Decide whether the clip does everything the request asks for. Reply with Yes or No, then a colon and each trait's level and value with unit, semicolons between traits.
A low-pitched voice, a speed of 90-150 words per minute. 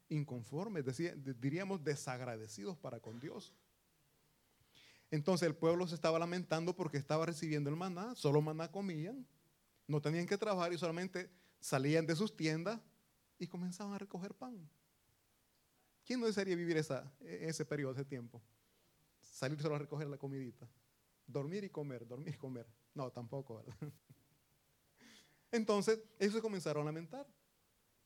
No: medium, 155 Hz; average, 140 wpm